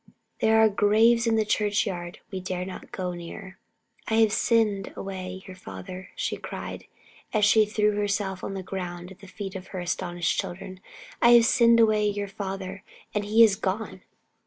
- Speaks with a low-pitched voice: No, high, 195 Hz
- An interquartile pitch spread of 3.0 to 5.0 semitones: No, narrow, 2.6 semitones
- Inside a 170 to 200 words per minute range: Yes, average, 180 wpm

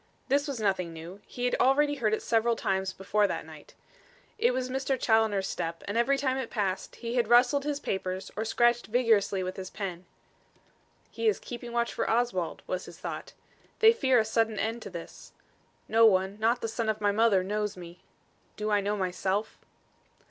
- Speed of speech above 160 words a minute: Yes, average, 190 wpm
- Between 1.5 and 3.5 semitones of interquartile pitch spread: No, average, 4.0 semitones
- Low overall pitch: No, high, 220 Hz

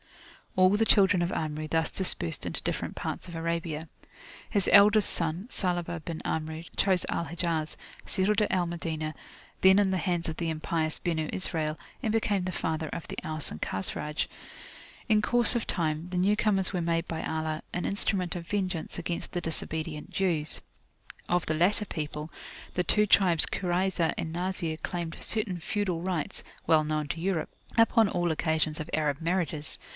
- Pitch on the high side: No, medium, 170 Hz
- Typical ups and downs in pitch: Yes, average, 3.1 semitones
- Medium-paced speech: Yes, average, 170 wpm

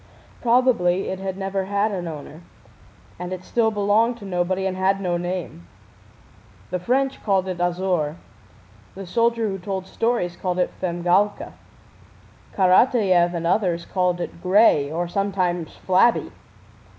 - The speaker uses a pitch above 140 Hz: Yes, medium, 185 Hz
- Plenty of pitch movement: No, narrow, 2.4 semitones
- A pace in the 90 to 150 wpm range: Yes, average, 140 wpm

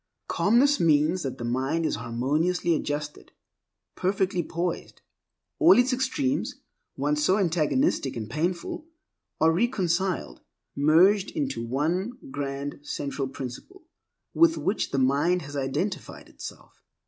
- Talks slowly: Yes, slow, 115 wpm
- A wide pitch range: Yes, wide, 6.0 semitones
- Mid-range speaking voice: Yes, medium, 165 Hz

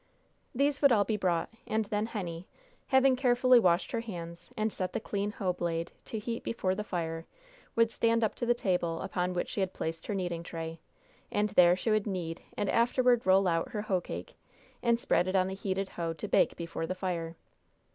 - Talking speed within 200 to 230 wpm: Yes, fast, 205 wpm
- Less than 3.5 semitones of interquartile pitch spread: No, average, 4.7 semitones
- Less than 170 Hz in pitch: No, high, 190 Hz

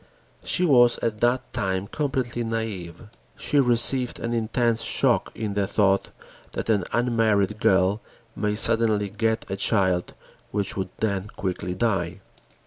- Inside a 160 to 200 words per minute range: No, slow, 135 wpm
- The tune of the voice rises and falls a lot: No, average, 3.3 semitones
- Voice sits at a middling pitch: No, low, 110 Hz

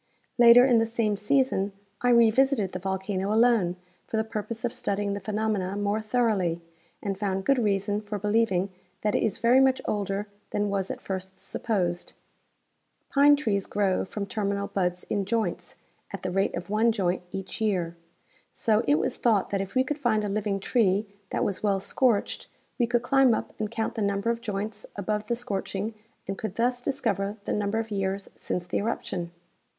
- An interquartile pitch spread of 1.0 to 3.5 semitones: Yes, average, 2.8 semitones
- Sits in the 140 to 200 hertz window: No, high, 210 Hz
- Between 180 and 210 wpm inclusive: Yes, average, 185 wpm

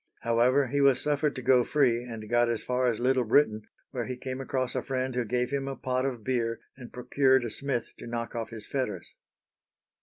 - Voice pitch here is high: No, low, 125 Hz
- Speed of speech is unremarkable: No, fast, 215 wpm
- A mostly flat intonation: Yes, narrow, 2.1 semitones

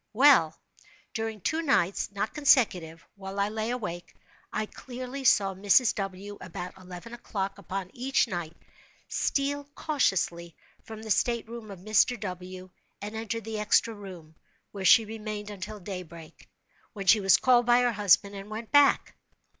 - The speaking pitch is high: Yes, high, 210 Hz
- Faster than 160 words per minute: No, average, 155 wpm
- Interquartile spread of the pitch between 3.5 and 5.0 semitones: Yes, average, 3.8 semitones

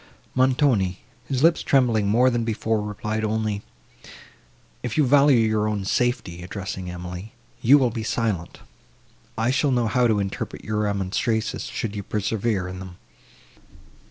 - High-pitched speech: No, low, 110 Hz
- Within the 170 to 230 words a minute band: No, average, 145 wpm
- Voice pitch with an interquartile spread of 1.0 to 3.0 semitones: No, average, 3.6 semitones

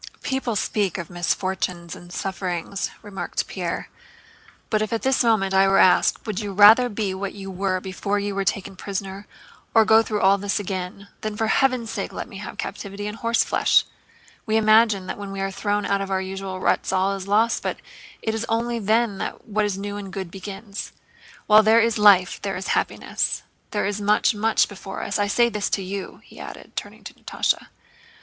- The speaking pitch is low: No, high, 200 Hz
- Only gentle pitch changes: Yes, narrow, 2.0 semitones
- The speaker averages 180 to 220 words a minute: Yes, average, 200 wpm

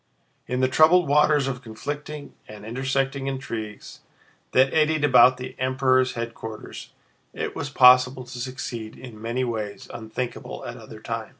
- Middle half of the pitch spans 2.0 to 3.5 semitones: Yes, narrow, 2.6 semitones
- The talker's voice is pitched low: Yes, low, 130 Hz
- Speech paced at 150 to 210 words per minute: No, average, 140 wpm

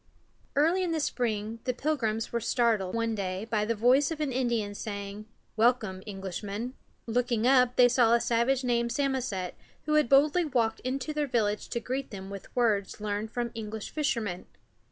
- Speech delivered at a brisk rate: No, average, 175 wpm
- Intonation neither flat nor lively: Yes, average, 3.5 semitones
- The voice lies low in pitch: No, high, 235 Hz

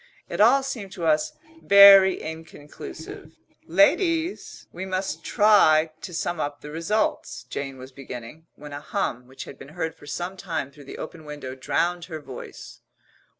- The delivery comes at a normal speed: Yes, average, 160 wpm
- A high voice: No, medium, 160 Hz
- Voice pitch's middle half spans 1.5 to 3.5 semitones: No, average, 4.6 semitones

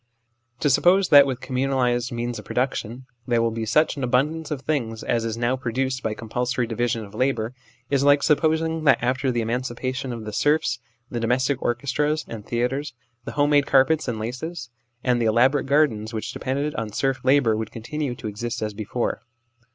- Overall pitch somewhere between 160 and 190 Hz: No, low, 125 Hz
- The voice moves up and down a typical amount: Yes, average, 3.3 semitones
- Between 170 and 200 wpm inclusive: Yes, average, 190 wpm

